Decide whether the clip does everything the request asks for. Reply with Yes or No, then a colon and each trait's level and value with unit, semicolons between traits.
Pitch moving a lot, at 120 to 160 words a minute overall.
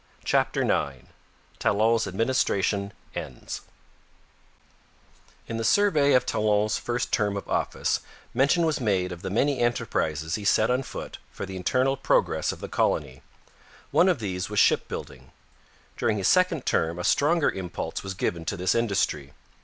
Yes: wide, 5.8 semitones; average, 150 wpm